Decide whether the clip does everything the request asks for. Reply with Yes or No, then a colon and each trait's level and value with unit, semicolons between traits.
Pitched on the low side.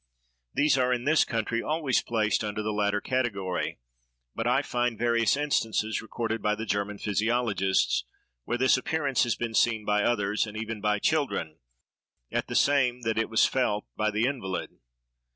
Yes: low, 115 Hz